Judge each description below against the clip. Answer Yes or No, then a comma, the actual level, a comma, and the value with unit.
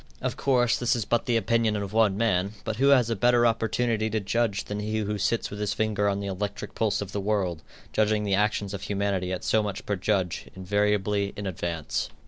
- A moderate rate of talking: No, fast, 220 wpm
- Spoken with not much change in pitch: Yes, narrow, 2.1 semitones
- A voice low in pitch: Yes, low, 105 Hz